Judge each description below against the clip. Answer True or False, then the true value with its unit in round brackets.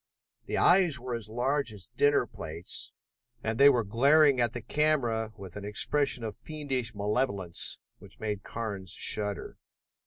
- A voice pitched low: True (115 Hz)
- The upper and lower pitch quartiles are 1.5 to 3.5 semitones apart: False (5.1 semitones)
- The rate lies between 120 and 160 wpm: True (150 wpm)